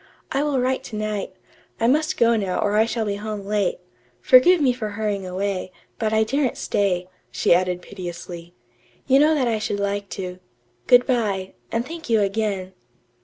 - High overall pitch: Yes, high, 215 Hz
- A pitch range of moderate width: Yes, average, 4.2 semitones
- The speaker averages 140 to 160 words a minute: No, average, 180 wpm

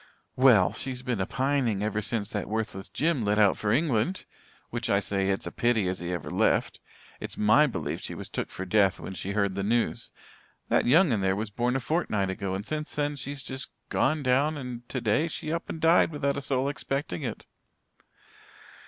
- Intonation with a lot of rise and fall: Yes, wide, 5.8 semitones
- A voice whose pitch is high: No, low, 120 Hz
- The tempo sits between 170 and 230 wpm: Yes, fast, 205 wpm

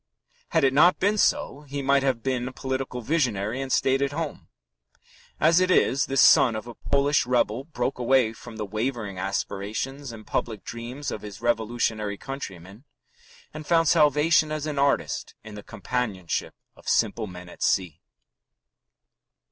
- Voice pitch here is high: No, low, 125 Hz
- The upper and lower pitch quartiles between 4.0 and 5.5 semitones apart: Yes, average, 4.5 semitones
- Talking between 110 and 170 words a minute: Yes, average, 160 wpm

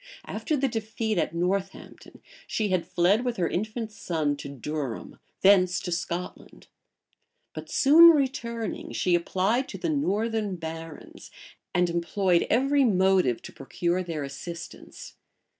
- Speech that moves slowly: Yes, slow, 130 wpm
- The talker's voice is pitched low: No, high, 190 Hz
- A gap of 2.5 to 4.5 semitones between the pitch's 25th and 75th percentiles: No, average, 4.9 semitones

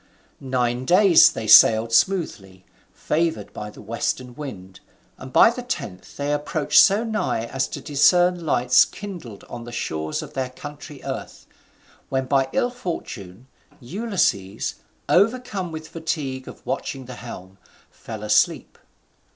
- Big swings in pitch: Yes, wide, 7.2 semitones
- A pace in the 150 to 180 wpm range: No, slow, 135 wpm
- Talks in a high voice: No, low, 130 Hz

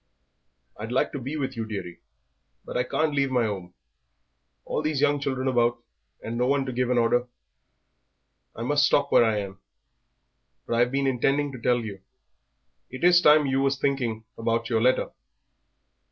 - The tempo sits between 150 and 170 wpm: No, average, 180 wpm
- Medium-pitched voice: No, low, 125 Hz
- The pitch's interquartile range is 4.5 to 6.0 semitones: No, average, 3.2 semitones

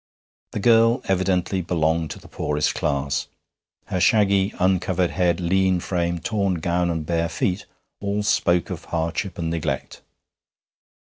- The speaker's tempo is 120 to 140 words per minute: Yes, slow, 135 wpm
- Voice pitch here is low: Yes, very low, 90 Hz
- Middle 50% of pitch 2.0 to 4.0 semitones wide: Yes, narrow, 2.6 semitones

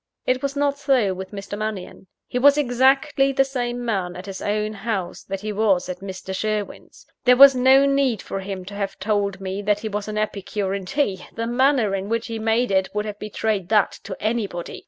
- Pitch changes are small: No, average, 4.2 semitones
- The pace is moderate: No, fast, 215 wpm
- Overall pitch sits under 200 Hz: No, high, 215 Hz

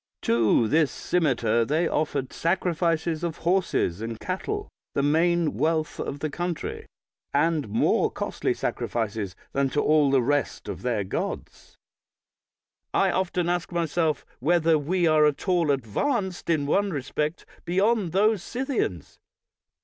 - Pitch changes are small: No, average, 4.1 semitones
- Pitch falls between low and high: Yes, medium, 160 Hz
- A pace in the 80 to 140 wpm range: Yes, slow, 135 wpm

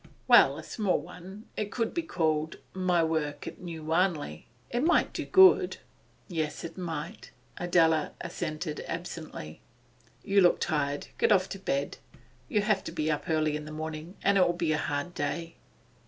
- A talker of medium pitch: Yes, medium, 165 Hz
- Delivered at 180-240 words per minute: No, average, 170 wpm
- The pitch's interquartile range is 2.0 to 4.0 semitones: Yes, average, 3.3 semitones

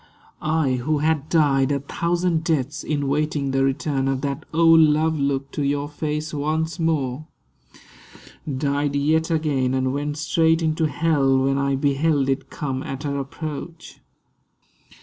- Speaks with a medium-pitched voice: Yes, medium, 145 Hz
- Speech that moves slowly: No, average, 150 wpm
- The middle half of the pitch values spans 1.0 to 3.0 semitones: Yes, narrow, 2.5 semitones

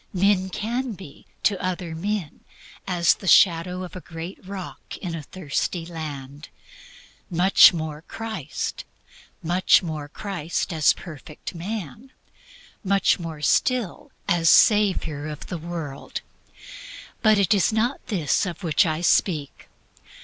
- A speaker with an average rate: No, slow, 130 wpm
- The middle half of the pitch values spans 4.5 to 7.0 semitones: No, average, 3.8 semitones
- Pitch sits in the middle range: Yes, medium, 175 Hz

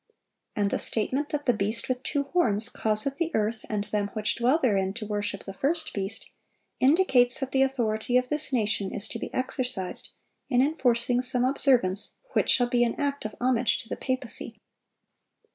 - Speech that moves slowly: No, average, 180 wpm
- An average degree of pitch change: Yes, average, 4.0 semitones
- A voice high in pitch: Yes, high, 245 Hz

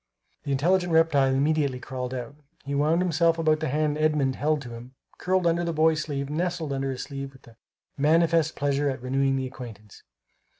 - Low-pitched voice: No, medium, 145 Hz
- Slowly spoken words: No, average, 180 wpm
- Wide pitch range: No, average, 3.2 semitones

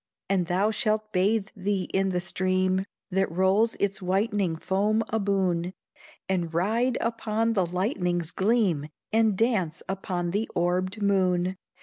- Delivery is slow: Yes, slow, 130 wpm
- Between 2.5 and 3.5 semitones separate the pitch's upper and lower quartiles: Yes, average, 2.9 semitones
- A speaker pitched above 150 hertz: Yes, high, 190 Hz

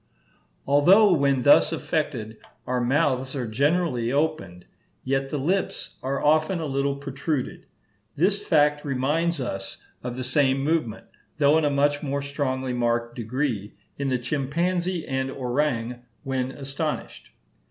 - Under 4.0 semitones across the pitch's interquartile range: Yes, average, 3.1 semitones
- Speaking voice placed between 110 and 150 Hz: Yes, medium, 140 Hz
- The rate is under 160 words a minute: Yes, slow, 135 wpm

